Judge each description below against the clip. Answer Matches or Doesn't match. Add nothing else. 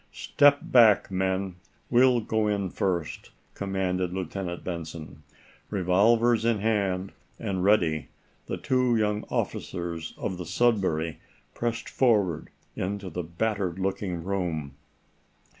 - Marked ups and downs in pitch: Doesn't match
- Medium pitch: Doesn't match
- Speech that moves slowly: Matches